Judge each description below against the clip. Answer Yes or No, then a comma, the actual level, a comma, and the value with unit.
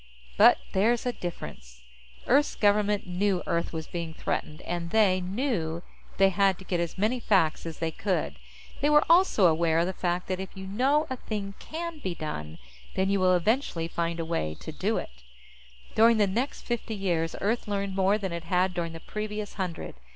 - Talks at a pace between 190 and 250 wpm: Yes, average, 195 wpm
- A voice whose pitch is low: No, high, 190 Hz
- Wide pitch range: No, average, 4.0 semitones